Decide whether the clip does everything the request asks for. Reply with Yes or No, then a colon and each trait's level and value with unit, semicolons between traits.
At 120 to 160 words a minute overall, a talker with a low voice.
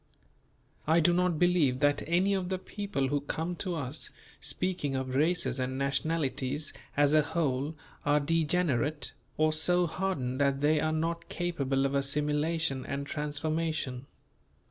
No: average, 145 wpm; medium, 150 Hz